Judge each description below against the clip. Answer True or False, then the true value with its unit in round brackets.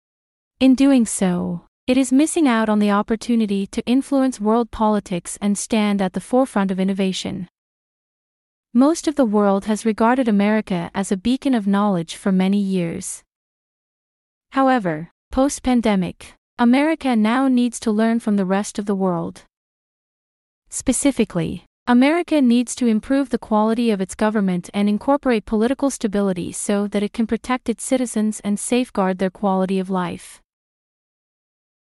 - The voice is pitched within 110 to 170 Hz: False (220 Hz)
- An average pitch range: True (4.1 semitones)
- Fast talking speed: False (145 wpm)